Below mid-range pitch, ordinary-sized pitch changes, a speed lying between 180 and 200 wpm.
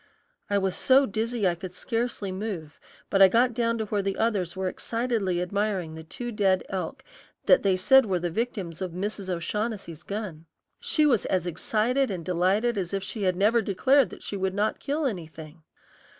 No: high, 200 Hz; average, 4.0 semitones; average, 185 wpm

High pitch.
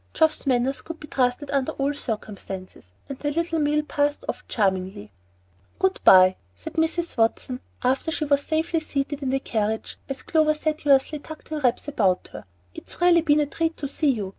Yes: very high, 280 Hz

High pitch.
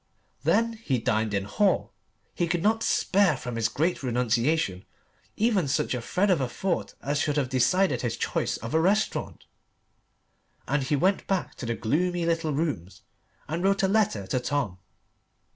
No: medium, 150 Hz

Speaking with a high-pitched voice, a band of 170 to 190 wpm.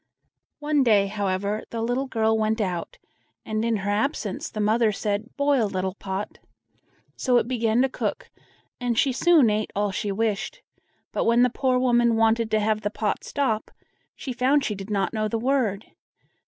Yes: high, 220 Hz; average, 180 wpm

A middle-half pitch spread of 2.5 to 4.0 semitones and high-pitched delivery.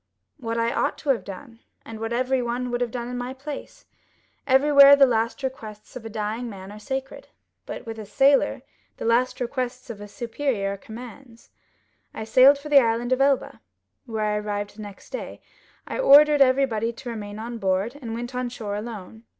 Yes: average, 3.1 semitones; high, 235 Hz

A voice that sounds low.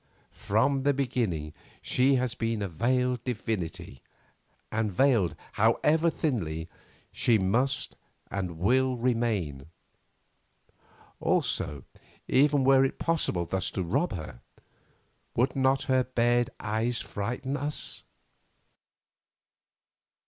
Yes: low, 120 Hz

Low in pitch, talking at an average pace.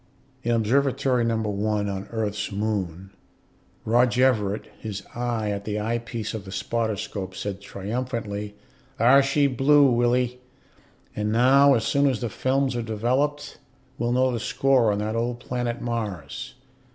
Yes: low, 115 Hz; average, 150 wpm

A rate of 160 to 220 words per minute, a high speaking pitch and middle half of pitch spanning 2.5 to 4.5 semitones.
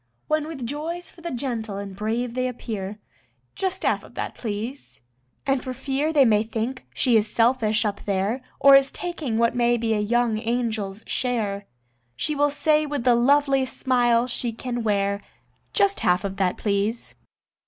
Yes: average, 175 wpm; high, 240 Hz; average, 4.1 semitones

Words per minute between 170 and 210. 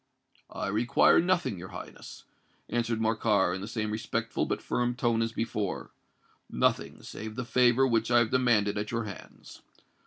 No: average, 155 wpm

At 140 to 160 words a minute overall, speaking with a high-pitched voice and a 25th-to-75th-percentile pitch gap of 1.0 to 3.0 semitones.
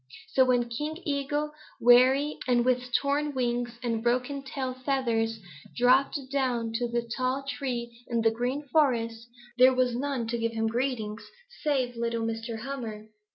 Yes: average, 155 wpm; high, 245 Hz; narrow, 2.6 semitones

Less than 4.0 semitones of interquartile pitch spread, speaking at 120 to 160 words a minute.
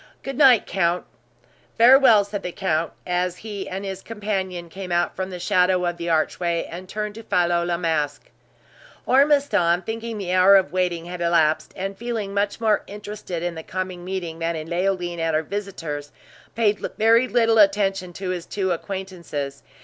No: average, 3.2 semitones; average, 170 wpm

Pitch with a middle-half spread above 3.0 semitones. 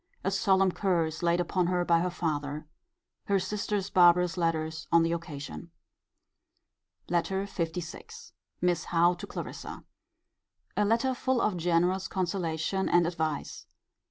No: narrow, 2.5 semitones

